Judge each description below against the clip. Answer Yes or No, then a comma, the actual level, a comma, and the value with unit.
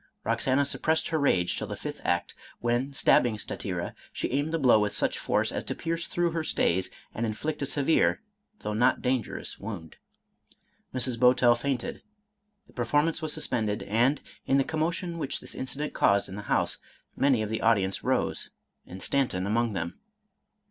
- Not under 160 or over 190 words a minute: Yes, average, 175 wpm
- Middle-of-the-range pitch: No, low, 125 Hz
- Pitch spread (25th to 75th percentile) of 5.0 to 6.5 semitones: Yes, average, 5.3 semitones